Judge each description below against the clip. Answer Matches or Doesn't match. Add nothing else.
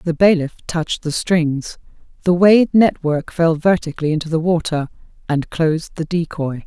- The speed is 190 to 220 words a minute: Doesn't match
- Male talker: Doesn't match